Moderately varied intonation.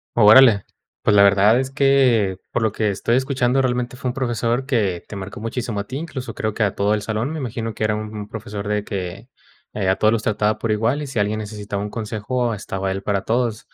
Yes: average, 3.2 semitones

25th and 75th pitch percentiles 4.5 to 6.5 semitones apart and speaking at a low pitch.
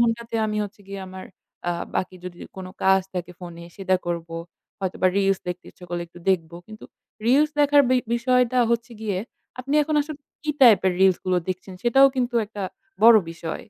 No: average, 4.8 semitones; high, 200 Hz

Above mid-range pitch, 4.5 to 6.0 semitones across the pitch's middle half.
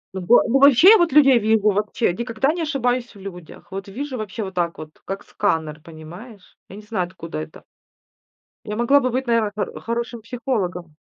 Yes: high, 215 Hz; average, 5.2 semitones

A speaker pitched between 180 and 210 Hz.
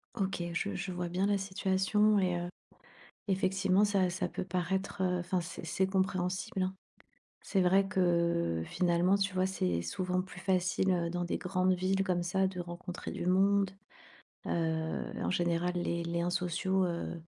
Yes: medium, 185 Hz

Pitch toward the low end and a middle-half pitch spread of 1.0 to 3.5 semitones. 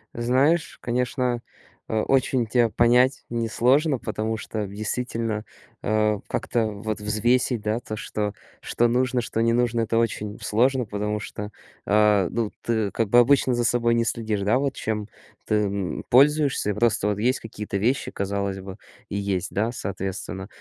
Yes: low, 110 Hz; average, 2.7 semitones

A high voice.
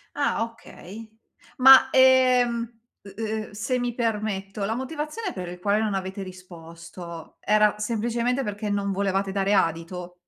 Yes: high, 210 Hz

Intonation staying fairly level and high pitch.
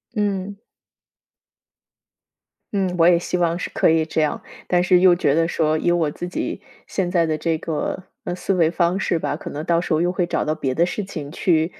No: narrow, 2.1 semitones; medium, 170 Hz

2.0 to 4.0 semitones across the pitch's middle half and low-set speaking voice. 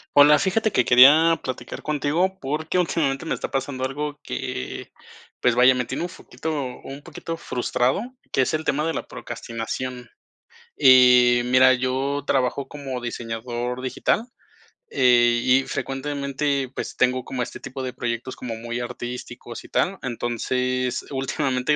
Yes: narrow, 2.5 semitones; low, 130 Hz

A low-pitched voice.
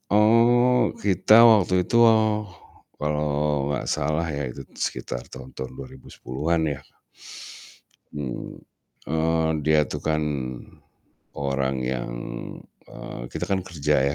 Yes: very low, 80 Hz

